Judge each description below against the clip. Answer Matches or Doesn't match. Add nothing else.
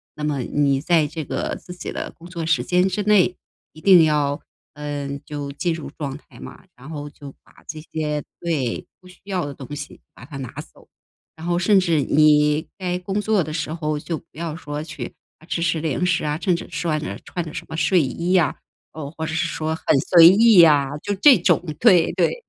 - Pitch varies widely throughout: Doesn't match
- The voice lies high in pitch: Doesn't match